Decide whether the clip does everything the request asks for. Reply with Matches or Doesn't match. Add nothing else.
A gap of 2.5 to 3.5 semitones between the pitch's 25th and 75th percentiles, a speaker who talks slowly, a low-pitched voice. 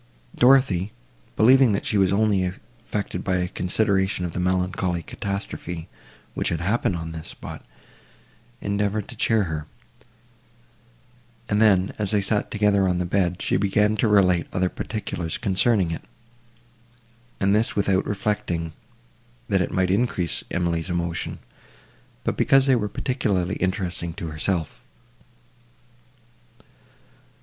Matches